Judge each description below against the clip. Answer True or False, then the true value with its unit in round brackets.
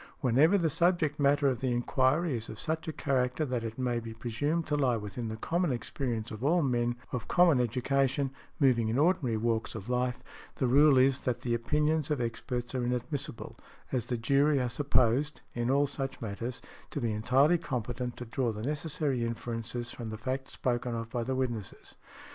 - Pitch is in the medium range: False (125 Hz)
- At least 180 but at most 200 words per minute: True (185 wpm)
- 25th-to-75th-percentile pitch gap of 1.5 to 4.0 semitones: True (3.3 semitones)